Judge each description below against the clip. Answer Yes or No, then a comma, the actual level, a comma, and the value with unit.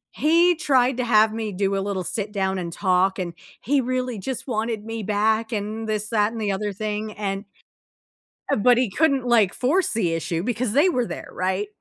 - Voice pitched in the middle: No, high, 215 Hz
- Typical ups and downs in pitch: Yes, average, 3.7 semitones